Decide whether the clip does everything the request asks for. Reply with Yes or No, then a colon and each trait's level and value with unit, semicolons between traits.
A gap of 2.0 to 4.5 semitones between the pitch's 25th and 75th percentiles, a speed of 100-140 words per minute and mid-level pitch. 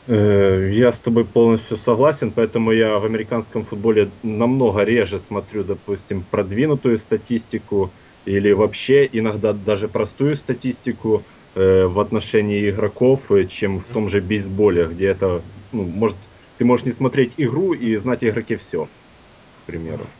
No: average, 2.7 semitones; average, 135 wpm; low, 110 Hz